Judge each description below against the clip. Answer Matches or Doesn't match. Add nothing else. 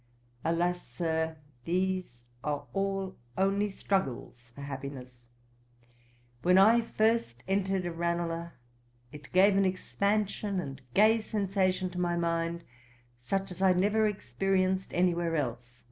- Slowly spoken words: Matches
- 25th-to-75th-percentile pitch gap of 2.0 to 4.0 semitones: Matches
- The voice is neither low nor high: Matches